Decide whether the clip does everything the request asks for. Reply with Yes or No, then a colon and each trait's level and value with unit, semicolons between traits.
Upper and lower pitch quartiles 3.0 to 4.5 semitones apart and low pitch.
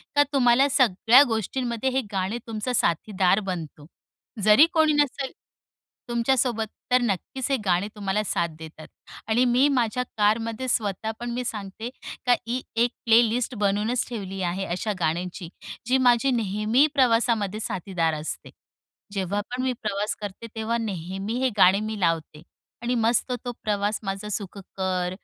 No: average, 4.2 semitones; high, 215 Hz